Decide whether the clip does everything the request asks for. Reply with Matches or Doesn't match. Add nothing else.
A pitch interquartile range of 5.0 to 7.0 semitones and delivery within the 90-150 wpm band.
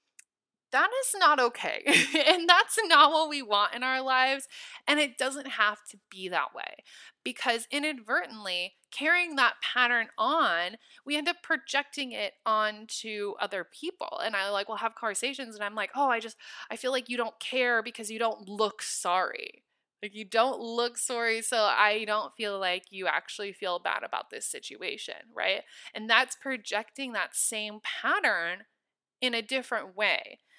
Doesn't match